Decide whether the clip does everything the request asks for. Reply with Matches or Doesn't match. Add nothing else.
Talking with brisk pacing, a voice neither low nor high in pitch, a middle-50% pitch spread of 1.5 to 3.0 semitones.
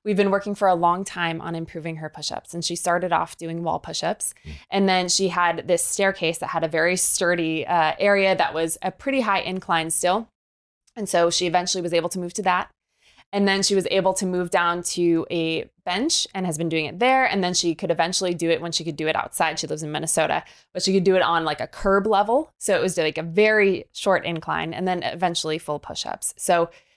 Matches